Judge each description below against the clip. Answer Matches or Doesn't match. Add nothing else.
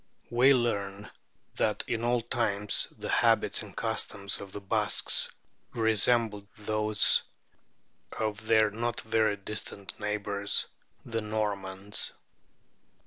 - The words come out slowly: Matches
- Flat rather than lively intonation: Matches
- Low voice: Matches